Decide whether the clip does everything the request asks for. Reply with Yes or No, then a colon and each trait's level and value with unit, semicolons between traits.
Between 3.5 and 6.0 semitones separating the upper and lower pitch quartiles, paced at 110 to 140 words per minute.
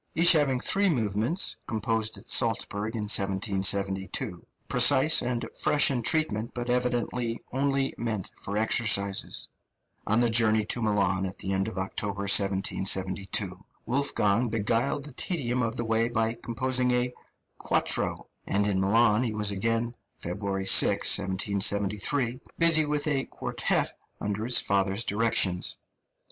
Yes: average, 3.8 semitones; slow, 135 wpm